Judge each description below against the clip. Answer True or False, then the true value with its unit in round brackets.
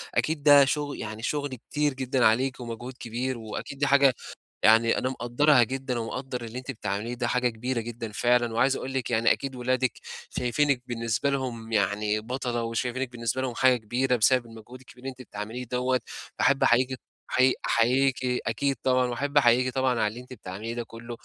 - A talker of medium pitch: False (125 Hz)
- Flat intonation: True (2.3 semitones)